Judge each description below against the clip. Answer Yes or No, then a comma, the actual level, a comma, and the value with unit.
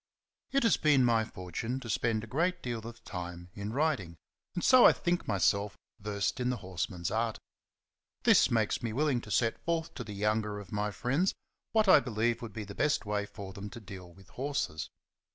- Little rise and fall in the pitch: No, average, 4.6 semitones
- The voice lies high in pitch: No, low, 110 Hz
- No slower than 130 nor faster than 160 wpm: No, average, 200 wpm